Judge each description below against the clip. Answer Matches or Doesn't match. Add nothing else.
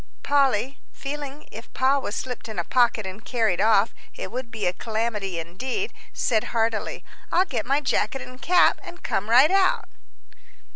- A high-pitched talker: Matches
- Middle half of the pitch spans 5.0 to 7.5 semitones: Doesn't match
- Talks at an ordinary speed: Matches